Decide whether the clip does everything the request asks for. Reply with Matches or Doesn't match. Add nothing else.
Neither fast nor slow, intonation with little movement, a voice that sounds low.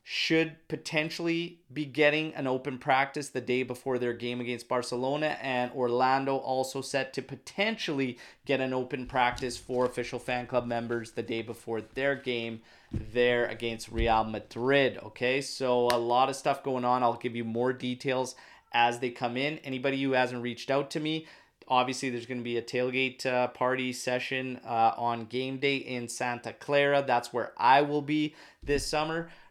Matches